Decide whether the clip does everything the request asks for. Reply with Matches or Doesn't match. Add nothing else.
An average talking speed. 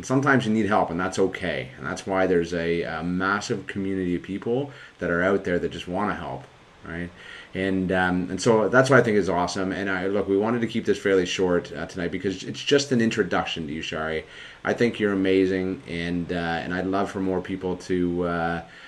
Doesn't match